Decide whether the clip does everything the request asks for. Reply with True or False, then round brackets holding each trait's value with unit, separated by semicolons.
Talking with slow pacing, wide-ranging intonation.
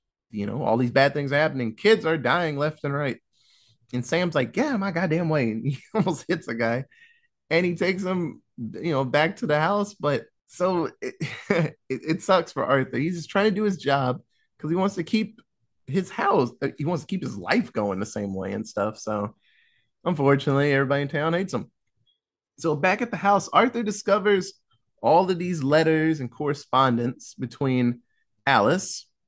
False (190 wpm; 6.3 semitones)